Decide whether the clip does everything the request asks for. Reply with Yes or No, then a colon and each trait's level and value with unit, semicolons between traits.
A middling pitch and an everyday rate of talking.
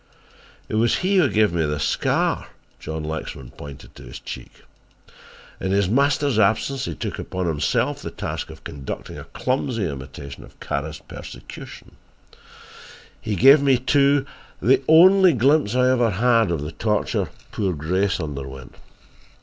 No: low, 105 Hz; average, 150 wpm